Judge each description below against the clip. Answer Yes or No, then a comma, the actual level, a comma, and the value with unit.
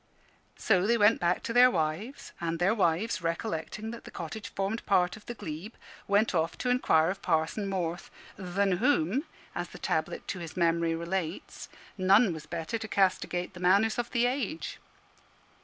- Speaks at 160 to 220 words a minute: Yes, average, 175 wpm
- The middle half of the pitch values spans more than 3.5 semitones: Yes, average, 4.7 semitones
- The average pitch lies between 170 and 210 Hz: Yes, high, 190 Hz